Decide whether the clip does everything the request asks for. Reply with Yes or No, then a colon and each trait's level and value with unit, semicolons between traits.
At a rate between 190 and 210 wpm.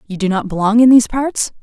No: fast, 260 wpm